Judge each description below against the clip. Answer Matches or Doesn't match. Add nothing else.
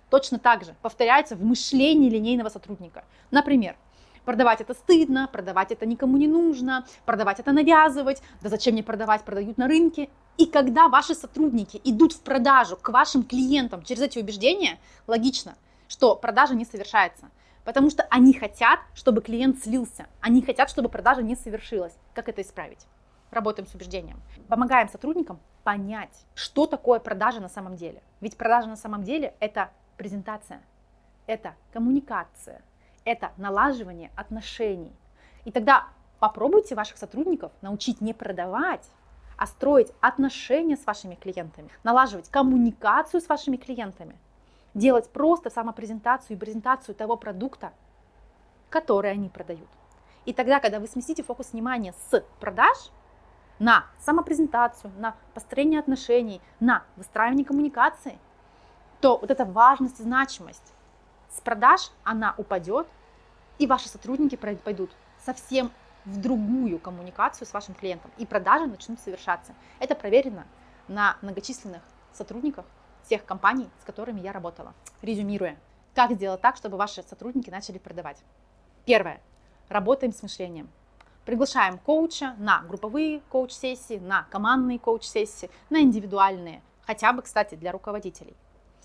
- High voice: Matches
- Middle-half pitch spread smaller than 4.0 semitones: Doesn't match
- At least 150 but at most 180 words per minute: Doesn't match